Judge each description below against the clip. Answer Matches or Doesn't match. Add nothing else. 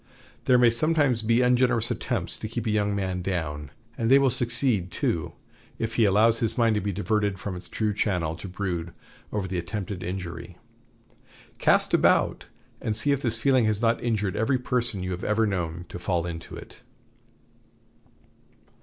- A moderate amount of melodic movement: Matches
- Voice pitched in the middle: Doesn't match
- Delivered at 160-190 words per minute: Matches